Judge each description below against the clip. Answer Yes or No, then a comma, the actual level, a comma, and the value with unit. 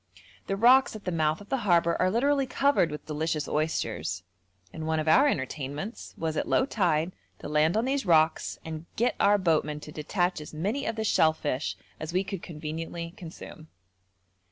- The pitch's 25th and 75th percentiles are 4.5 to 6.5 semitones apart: Yes, average, 5.0 semitones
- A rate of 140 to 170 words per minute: No, average, 180 wpm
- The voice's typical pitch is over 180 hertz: No, medium, 165 Hz